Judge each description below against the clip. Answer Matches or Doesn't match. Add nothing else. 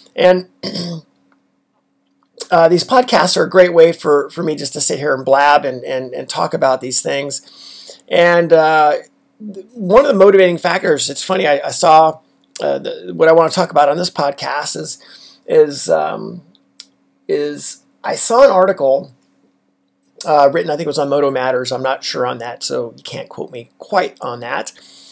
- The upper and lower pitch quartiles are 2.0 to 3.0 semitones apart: Doesn't match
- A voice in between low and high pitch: Matches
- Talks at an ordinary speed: Matches